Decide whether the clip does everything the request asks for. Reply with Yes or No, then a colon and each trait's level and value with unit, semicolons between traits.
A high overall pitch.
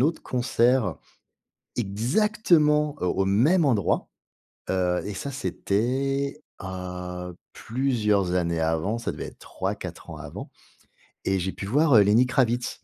No: low, 115 Hz